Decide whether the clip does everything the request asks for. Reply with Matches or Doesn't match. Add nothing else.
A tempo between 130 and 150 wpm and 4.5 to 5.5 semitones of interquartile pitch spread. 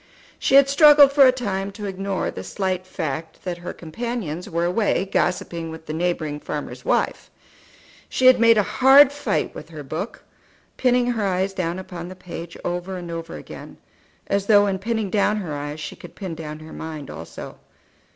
Doesn't match